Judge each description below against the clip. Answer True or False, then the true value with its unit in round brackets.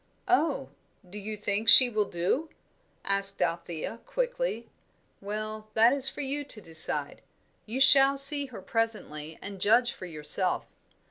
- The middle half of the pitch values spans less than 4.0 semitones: False (5.6 semitones)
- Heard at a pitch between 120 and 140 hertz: False (215 Hz)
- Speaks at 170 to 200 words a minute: False (140 wpm)